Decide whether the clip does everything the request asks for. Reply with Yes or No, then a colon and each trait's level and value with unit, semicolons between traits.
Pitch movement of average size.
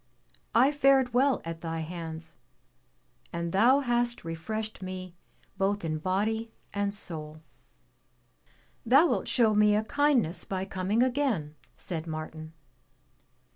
No: wide, 6.4 semitones